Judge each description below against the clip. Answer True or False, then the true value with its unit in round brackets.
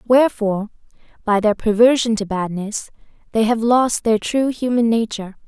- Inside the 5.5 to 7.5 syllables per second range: False (5.1 syllables/s)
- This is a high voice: True (225 Hz)